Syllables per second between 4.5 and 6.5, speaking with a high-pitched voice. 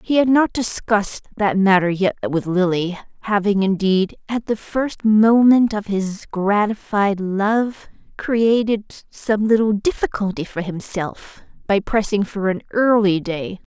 No: 3.9 syllables/s; high, 205 Hz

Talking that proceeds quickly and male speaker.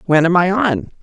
No: fast, 235 wpm; female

